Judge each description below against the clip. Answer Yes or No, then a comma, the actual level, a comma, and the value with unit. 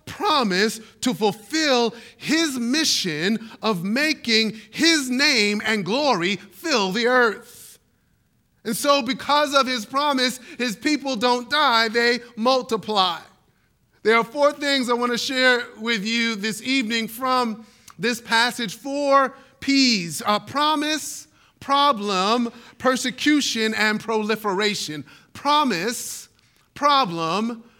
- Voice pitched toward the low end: No, high, 240 Hz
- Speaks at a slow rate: Yes, slow, 110 wpm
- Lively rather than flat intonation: No, average, 3.8 semitones